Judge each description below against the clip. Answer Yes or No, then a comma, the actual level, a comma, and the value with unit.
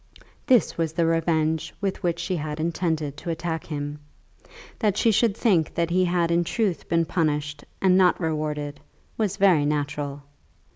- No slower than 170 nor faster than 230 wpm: No, average, 160 wpm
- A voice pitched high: No, medium, 165 Hz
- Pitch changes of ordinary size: Yes, average, 3.3 semitones